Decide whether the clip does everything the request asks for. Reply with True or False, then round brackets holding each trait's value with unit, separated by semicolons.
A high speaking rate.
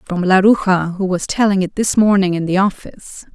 False (195 wpm)